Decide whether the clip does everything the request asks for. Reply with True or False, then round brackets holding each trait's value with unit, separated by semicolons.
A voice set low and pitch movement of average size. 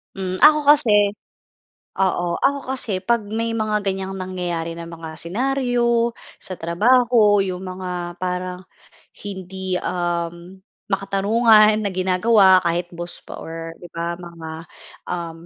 False (185 Hz; 3.7 semitones)